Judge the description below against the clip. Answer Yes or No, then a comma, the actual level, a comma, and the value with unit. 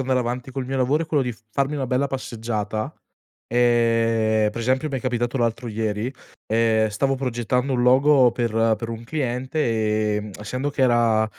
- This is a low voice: Yes, low, 120 Hz